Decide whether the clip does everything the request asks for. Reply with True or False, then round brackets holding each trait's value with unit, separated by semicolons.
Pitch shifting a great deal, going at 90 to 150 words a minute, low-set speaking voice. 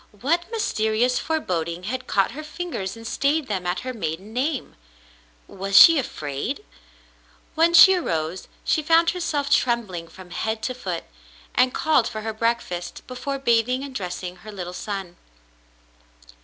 False (7.4 semitones; 145 wpm; 230 Hz)